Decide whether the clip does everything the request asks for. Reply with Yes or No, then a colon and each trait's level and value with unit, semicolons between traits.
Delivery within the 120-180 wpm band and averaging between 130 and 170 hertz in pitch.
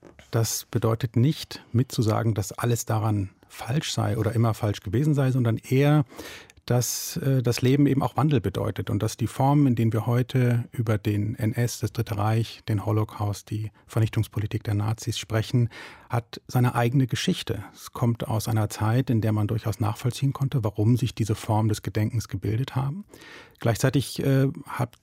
No: average, 170 wpm; low, 115 Hz